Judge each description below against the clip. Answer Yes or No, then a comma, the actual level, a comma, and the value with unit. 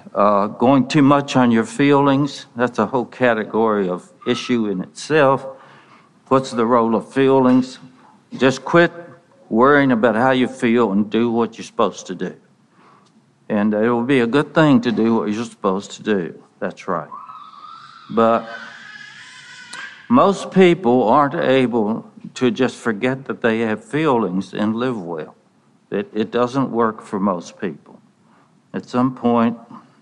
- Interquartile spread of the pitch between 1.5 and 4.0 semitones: Yes, average, 3.2 semitones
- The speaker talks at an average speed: Yes, average, 150 wpm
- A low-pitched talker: Yes, low, 125 Hz